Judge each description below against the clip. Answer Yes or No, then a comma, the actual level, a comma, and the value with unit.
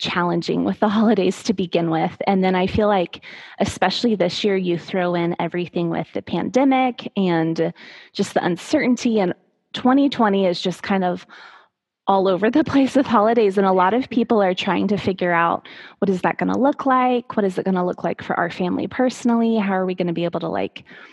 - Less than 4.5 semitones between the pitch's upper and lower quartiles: No, average, 4.8 semitones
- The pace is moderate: No, fast, 215 wpm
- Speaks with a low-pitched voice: No, high, 195 Hz